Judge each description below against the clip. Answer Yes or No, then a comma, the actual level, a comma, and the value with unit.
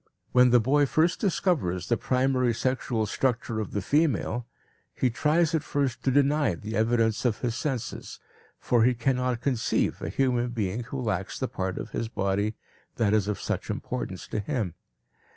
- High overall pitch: No, low, 120 Hz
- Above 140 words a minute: Yes, average, 170 wpm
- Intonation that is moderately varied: Yes, average, 3.6 semitones